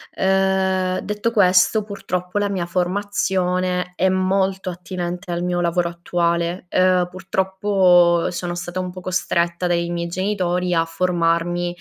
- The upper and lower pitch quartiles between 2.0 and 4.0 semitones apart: No, narrow, 1.5 semitones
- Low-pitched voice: No, medium, 180 Hz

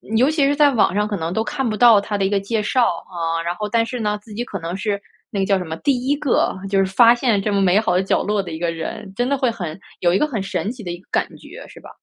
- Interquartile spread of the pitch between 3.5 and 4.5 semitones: Yes, average, 4.2 semitones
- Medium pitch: No, high, 205 Hz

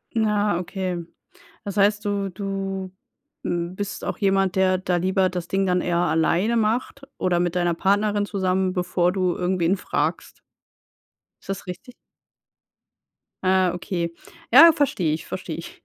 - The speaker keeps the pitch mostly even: Yes, narrow, 2.2 semitones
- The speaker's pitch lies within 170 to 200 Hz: Yes, high, 190 Hz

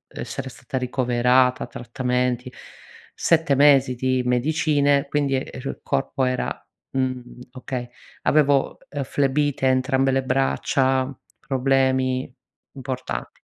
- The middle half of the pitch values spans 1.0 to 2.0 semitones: Yes, narrow, 1.5 semitones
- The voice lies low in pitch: Yes, low, 130 Hz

